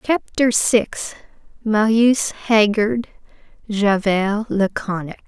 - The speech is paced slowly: Yes, slow, 55 wpm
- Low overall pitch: No, high, 215 Hz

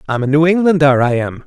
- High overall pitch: No, medium, 145 Hz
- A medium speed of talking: No, fast, 245 wpm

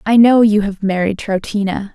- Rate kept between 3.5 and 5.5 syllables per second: Yes, 4.9 syllables/s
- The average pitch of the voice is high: Yes, high, 205 Hz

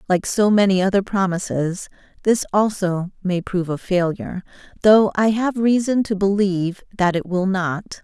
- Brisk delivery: No, average, 155 wpm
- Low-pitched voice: No, high, 195 Hz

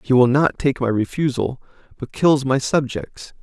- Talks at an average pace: Yes, average, 175 wpm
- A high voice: No, low, 130 Hz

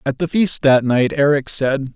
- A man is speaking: Yes, male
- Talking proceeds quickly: Yes, fast, 215 wpm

